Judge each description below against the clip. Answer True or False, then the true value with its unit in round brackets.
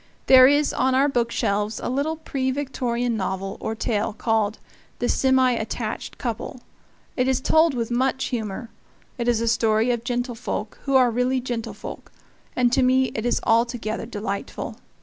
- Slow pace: False (165 wpm)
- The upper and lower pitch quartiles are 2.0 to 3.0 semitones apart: True (2.7 semitones)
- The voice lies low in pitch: False (245 Hz)